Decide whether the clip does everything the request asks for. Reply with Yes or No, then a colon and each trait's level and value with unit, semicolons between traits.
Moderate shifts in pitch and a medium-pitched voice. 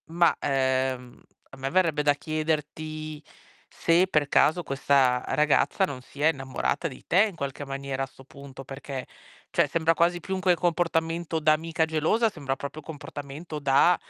Yes: average, 3.3 semitones; medium, 150 Hz